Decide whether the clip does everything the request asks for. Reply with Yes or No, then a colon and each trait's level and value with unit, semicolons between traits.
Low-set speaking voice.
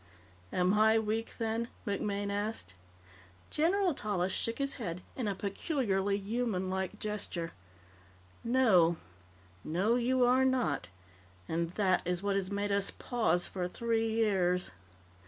No: high, 205 Hz